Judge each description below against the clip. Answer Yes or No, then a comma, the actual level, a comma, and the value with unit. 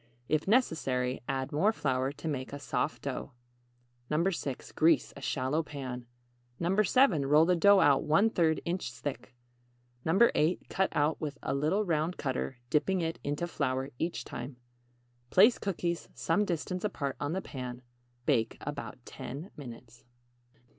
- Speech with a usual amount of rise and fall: Yes, average, 4.7 semitones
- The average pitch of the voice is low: No, medium, 150 Hz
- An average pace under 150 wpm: Yes, average, 140 wpm